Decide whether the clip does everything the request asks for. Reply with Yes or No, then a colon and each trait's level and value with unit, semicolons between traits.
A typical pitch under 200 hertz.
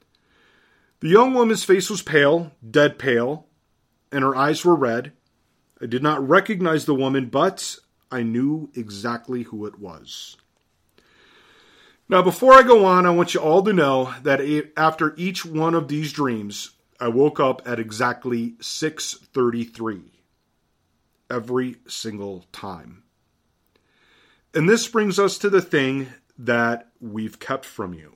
Yes: medium, 140 Hz